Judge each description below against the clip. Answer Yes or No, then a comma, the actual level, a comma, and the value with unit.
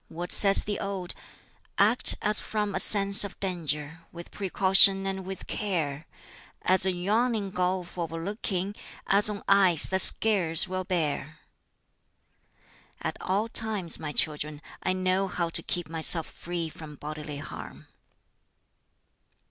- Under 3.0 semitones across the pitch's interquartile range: No, average, 3.3 semitones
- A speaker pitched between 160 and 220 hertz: Yes, medium, 185 Hz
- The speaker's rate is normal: No, slow, 130 wpm